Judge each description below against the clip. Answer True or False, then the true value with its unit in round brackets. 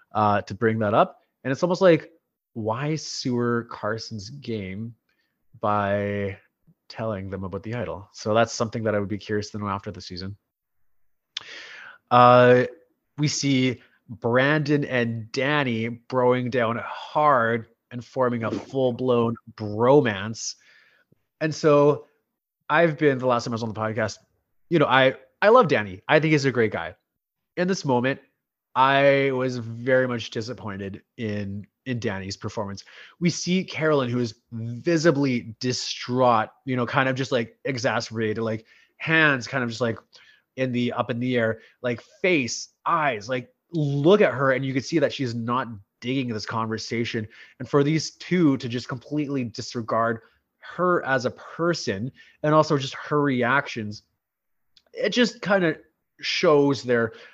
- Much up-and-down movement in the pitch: False (3.8 semitones)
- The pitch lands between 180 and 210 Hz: False (125 Hz)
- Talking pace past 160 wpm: False (155 wpm)